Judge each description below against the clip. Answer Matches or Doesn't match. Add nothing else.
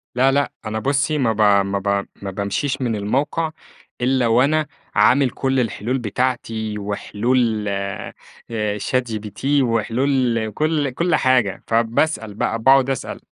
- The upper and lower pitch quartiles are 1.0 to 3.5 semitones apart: Doesn't match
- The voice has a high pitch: Doesn't match